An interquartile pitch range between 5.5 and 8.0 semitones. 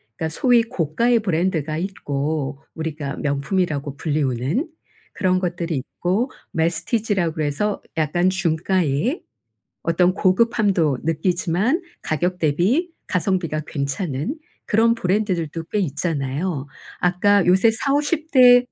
No: average, 5.1 semitones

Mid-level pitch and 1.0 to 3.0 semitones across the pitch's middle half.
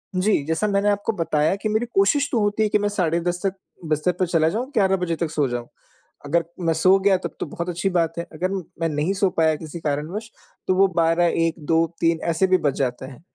No: medium, 170 Hz; average, 3.4 semitones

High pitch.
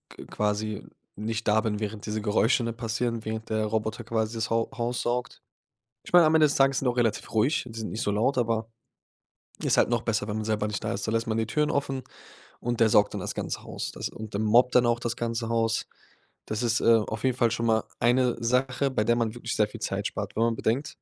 No: low, 115 Hz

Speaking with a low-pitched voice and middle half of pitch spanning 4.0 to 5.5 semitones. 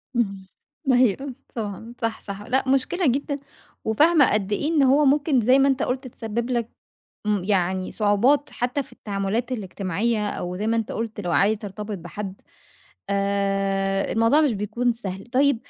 No: high, 225 Hz; average, 4.5 semitones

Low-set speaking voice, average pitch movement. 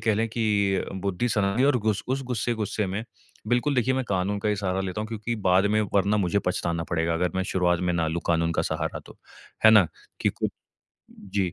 Yes: low, 100 Hz; average, 3.3 semitones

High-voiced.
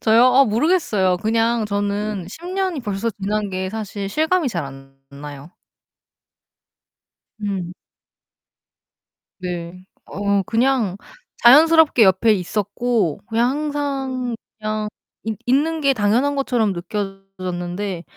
Yes: high, 215 Hz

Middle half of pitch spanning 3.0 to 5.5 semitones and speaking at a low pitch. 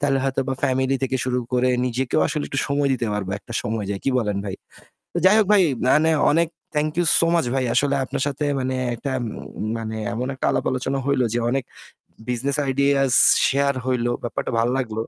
No: narrow, 2.5 semitones; low, 130 Hz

